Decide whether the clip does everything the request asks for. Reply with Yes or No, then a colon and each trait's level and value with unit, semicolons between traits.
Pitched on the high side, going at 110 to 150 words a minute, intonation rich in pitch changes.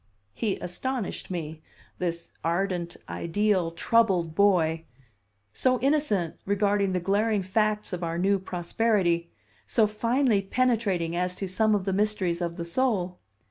No: high, 195 Hz; slow, 135 wpm; average, 3.6 semitones